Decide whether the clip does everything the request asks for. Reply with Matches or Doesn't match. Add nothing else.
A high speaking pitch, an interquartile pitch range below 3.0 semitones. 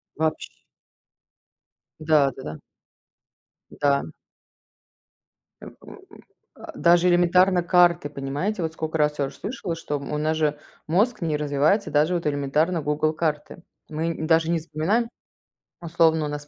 Doesn't match